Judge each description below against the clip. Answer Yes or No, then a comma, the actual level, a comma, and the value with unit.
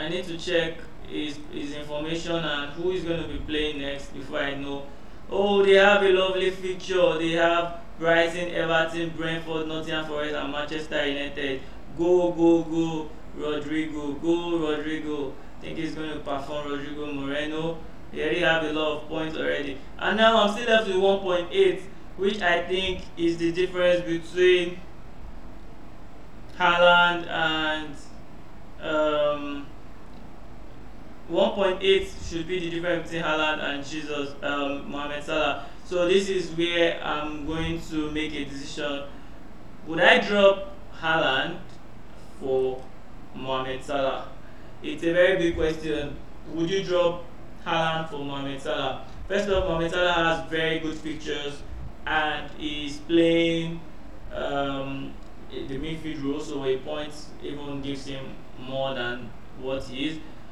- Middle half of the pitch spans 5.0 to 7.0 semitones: No, average, 2.9 semitones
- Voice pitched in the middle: Yes, medium, 155 Hz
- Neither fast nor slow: Yes, average, 145 wpm